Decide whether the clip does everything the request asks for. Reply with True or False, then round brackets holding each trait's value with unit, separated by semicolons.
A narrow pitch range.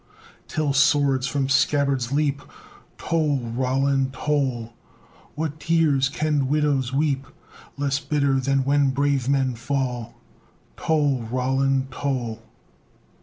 True (1.7 semitones)